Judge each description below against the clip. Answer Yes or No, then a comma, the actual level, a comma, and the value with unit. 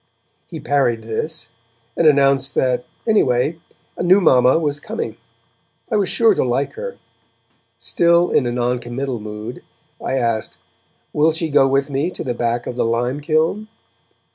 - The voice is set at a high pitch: No, low, 135 Hz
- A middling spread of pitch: Yes, average, 4.9 semitones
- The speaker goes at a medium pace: Yes, average, 155 wpm